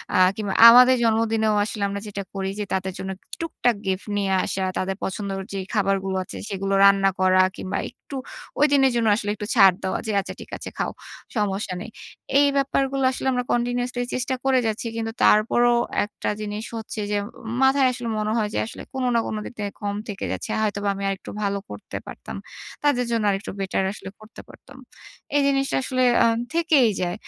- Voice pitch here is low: No, high, 215 Hz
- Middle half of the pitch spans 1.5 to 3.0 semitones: No, average, 4.0 semitones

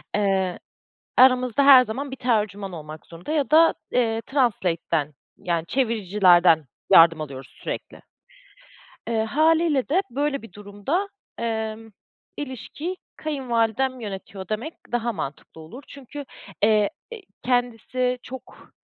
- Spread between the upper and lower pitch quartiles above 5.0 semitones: Yes, wide, 5.5 semitones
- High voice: Yes, high, 230 Hz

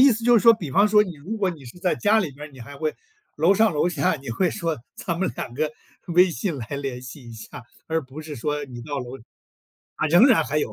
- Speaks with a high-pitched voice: No, medium, 155 Hz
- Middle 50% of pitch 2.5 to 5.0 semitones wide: No, wide, 5.6 semitones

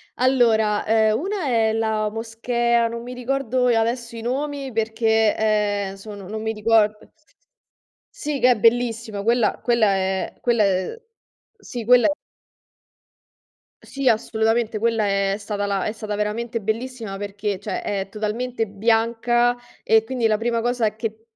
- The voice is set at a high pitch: Yes, high, 225 Hz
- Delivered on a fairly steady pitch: Yes, narrow, 2.1 semitones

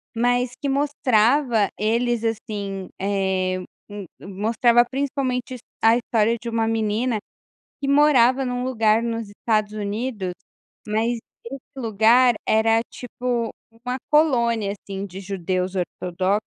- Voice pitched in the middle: No, high, 225 Hz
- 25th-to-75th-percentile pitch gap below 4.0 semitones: Yes, average, 3.3 semitones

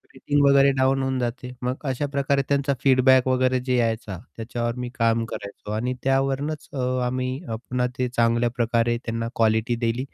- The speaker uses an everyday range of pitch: No, narrow, 2.2 semitones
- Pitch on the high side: No, low, 125 Hz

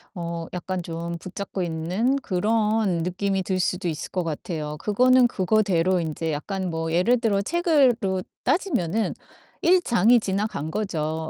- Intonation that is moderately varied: Yes, average, 4.5 semitones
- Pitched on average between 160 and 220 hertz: Yes, medium, 185 Hz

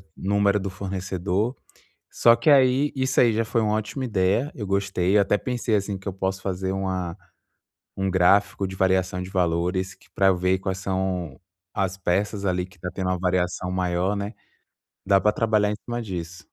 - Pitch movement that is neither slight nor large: No, narrow, 2.1 semitones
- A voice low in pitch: Yes, very low, 95 Hz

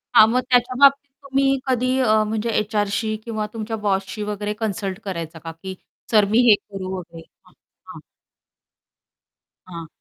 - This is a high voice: Yes, high, 215 Hz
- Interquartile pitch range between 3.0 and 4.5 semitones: Yes, average, 3.6 semitones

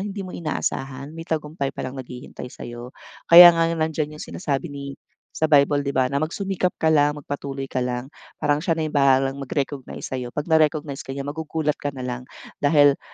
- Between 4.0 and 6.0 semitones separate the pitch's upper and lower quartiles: No, average, 2.8 semitones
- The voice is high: No, medium, 145 Hz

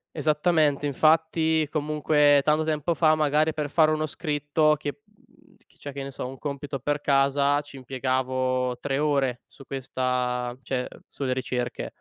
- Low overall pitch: No, medium, 145 Hz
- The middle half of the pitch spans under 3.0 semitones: Yes, narrow, 2.6 semitones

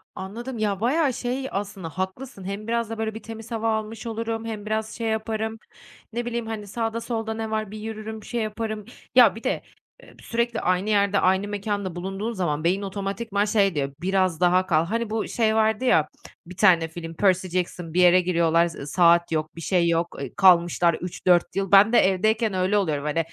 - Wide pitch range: No, average, 3.7 semitones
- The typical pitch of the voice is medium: No, high, 205 Hz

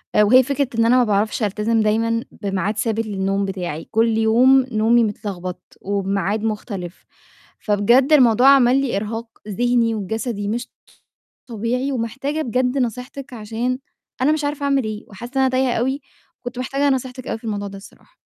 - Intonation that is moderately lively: Yes, average, 3.5 semitones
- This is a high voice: Yes, high, 230 Hz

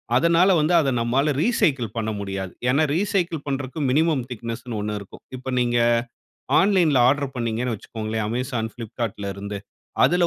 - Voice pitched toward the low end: Yes, low, 125 Hz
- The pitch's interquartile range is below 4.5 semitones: No, wide, 5.6 semitones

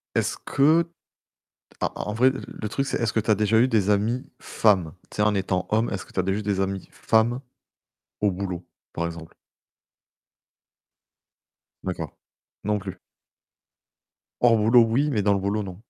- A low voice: Yes, low, 105 Hz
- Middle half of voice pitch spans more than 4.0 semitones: No, average, 2.9 semitones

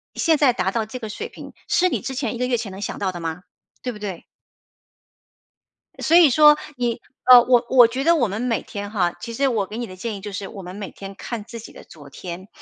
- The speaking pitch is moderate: No, high, 225 Hz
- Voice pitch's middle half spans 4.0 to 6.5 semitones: Yes, average, 4.3 semitones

